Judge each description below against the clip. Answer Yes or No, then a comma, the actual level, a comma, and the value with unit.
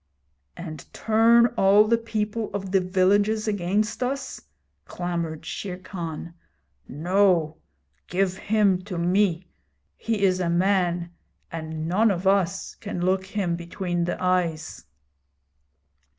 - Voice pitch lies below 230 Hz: Yes, medium, 185 Hz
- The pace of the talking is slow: Yes, slow, 120 wpm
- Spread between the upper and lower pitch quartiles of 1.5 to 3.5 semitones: Yes, average, 2.9 semitones